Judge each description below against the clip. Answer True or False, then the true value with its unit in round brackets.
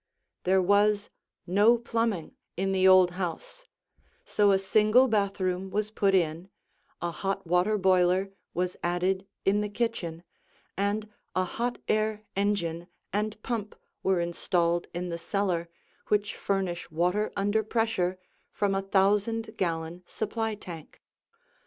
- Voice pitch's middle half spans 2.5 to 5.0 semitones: True (2.9 semitones)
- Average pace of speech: False (130 wpm)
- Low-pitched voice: False (195 Hz)